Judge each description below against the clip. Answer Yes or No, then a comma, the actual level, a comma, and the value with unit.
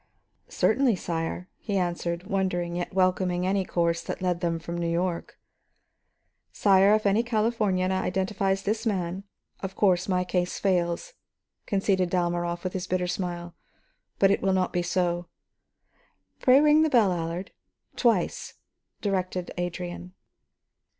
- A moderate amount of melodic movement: No, narrow, 2.0 semitones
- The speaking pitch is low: No, medium, 185 Hz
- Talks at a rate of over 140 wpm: No, slow, 135 wpm